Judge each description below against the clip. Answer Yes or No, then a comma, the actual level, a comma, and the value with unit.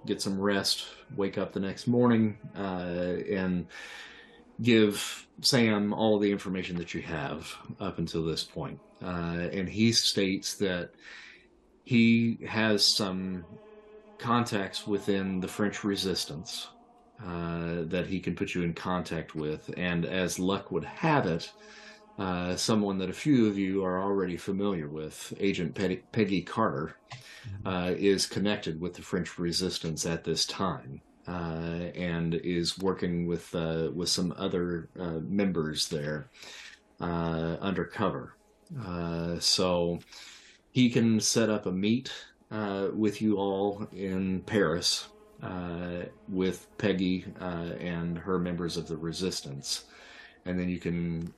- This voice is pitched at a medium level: No, very low, 95 Hz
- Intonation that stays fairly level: No, average, 3.0 semitones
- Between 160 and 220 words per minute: No, slow, 135 wpm